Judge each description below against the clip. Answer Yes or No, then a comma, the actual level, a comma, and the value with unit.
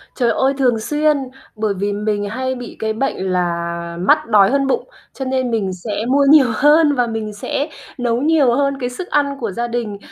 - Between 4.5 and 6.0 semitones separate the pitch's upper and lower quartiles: Yes, average, 4.8 semitones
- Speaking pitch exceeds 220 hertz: Yes, high, 240 Hz